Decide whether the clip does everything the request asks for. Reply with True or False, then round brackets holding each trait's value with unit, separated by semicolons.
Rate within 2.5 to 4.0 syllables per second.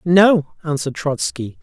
False (4.2 syllables/s)